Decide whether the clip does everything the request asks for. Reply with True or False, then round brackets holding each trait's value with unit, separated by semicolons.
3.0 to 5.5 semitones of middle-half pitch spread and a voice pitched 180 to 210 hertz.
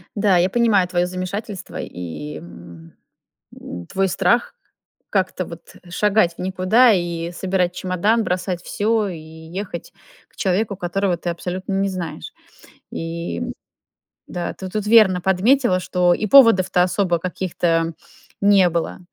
False (2.5 semitones; 185 Hz)